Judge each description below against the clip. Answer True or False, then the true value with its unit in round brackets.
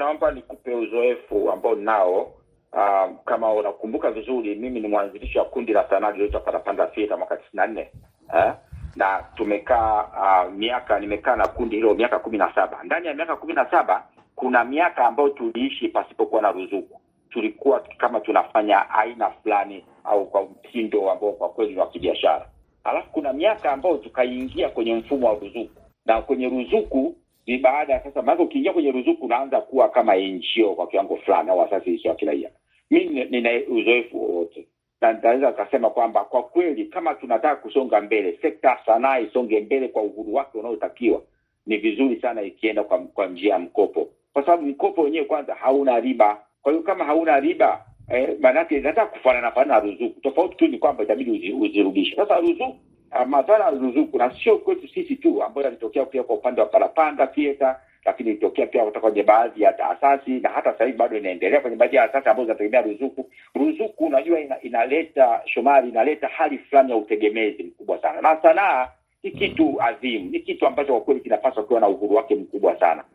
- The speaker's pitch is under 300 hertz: False (320 Hz)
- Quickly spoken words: True (165 wpm)